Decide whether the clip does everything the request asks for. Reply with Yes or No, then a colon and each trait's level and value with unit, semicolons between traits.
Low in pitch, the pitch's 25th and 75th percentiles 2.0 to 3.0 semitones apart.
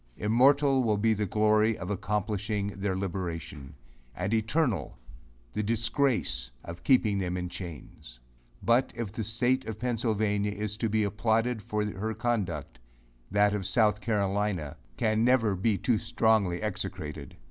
Yes: low, 105 Hz; narrow, 2.6 semitones